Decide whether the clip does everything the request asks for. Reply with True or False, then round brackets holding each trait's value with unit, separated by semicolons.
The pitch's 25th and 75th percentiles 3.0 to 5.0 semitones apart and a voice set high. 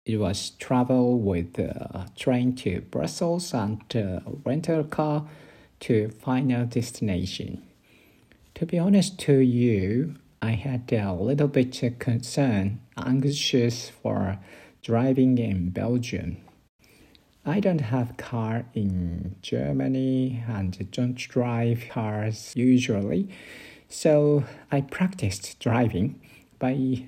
False (4.0 semitones; 120 Hz)